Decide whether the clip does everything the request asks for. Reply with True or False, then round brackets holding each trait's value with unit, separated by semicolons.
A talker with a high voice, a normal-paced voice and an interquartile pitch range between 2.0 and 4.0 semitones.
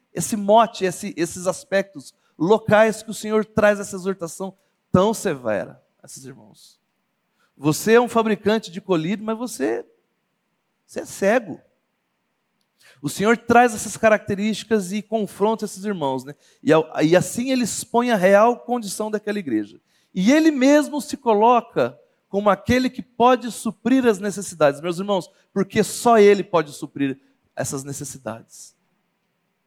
True (205 Hz; 140 wpm; 3.7 semitones)